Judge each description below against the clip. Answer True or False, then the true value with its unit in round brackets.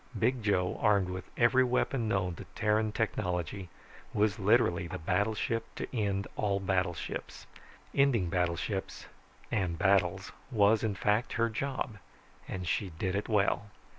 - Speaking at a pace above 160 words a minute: False (135 wpm)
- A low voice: True (100 Hz)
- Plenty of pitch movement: False (3.2 semitones)